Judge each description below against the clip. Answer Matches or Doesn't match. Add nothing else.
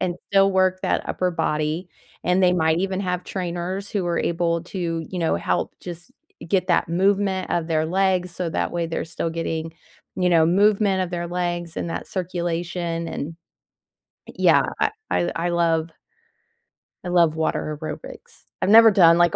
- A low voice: Doesn't match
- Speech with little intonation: Matches